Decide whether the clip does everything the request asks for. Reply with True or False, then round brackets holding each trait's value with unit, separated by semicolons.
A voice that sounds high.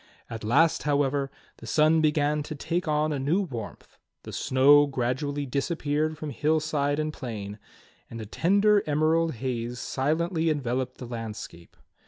False (145 Hz)